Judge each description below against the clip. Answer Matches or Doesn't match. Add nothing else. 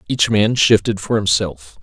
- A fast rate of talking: Doesn't match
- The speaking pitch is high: Doesn't match